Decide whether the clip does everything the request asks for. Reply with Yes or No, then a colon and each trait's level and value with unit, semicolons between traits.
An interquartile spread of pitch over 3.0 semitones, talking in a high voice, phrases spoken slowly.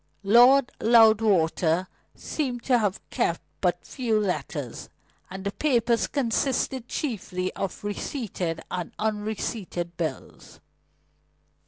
Yes: average, 4.8 semitones; high, 215 Hz; slow, 100 wpm